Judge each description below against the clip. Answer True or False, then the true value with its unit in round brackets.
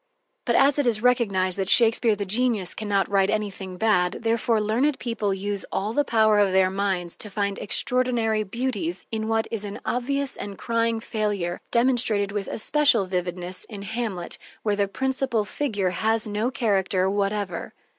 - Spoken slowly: False (165 wpm)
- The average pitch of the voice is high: True (210 Hz)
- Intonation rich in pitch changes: False (3.0 semitones)